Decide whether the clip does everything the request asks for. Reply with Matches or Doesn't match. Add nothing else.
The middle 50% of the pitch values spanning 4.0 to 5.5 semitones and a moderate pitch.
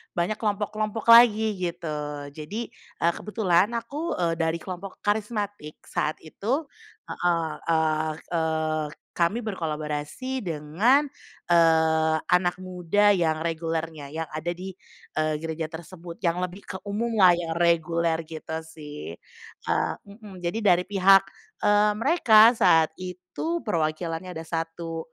Matches